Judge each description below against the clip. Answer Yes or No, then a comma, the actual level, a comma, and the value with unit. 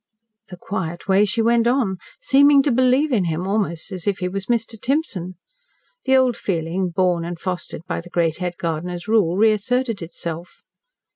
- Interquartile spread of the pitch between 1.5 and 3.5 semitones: No, average, 5.1 semitones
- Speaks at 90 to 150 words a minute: No, average, 170 wpm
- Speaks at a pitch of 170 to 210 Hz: Yes, high, 190 Hz